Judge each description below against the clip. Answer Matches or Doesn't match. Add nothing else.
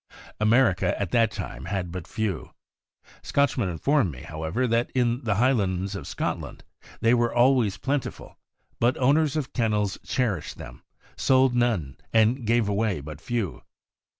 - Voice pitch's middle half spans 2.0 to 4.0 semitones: Doesn't match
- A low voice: Matches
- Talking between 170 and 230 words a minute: Doesn't match